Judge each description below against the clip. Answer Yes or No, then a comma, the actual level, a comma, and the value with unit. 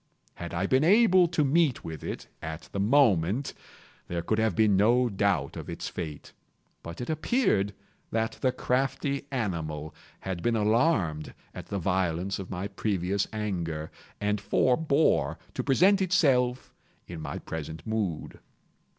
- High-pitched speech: No, low, 105 Hz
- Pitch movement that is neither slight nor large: No, wide, 7.2 semitones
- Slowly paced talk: No, average, 145 wpm